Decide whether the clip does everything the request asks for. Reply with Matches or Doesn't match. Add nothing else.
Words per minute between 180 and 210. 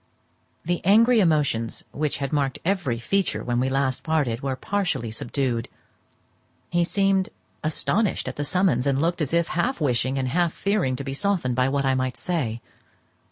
Doesn't match